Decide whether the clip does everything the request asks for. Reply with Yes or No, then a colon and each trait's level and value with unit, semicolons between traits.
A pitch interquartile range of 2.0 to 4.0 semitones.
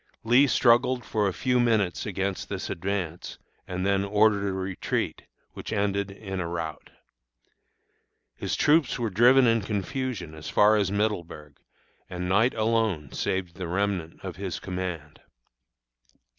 Yes: average, 3.6 semitones